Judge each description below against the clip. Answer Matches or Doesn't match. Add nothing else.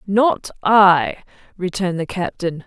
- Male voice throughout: Doesn't match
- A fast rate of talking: Doesn't match